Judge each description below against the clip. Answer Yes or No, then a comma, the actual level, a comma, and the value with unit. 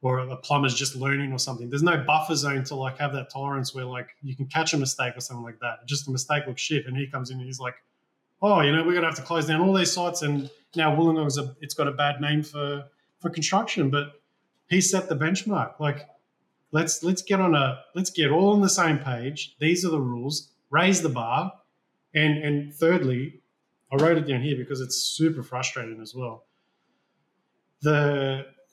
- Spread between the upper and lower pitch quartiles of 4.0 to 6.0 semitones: No, average, 3.4 semitones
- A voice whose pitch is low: No, medium, 145 Hz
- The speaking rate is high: Yes, fast, 215 wpm